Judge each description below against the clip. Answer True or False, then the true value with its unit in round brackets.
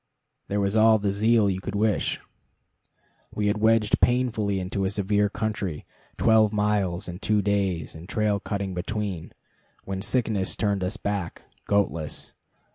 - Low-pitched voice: True (100 Hz)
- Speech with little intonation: True (2.0 semitones)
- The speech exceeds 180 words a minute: False (145 wpm)